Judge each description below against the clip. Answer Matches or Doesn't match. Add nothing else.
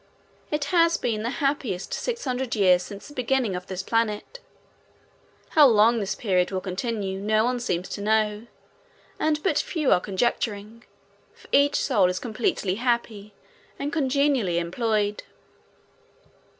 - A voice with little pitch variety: Doesn't match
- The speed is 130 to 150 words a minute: Matches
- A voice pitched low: Doesn't match